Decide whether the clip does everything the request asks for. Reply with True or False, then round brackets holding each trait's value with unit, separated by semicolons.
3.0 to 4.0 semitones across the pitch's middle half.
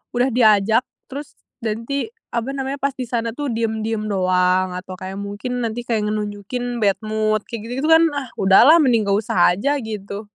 True (3.5 semitones)